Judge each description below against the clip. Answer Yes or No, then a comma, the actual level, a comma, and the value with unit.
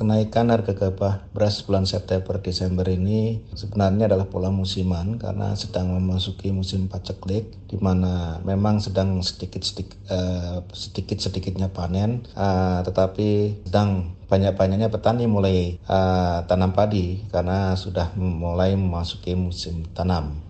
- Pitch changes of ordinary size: No, narrow, 1.7 semitones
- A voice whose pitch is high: No, very low, 95 Hz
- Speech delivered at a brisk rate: No, average, 105 wpm